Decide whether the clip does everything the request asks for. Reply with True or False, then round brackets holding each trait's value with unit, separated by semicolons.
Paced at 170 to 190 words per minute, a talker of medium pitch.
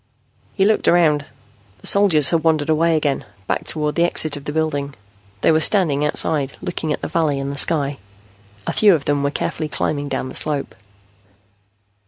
True (185 wpm; 150 Hz)